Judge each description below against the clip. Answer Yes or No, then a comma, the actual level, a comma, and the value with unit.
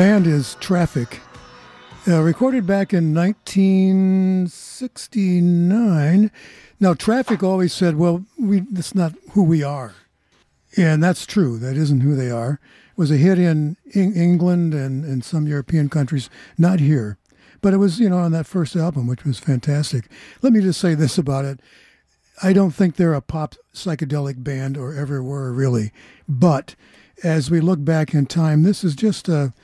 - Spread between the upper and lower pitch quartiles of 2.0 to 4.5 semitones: No, average, 5.0 semitones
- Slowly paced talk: No, average, 170 wpm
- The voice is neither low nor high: Yes, medium, 165 Hz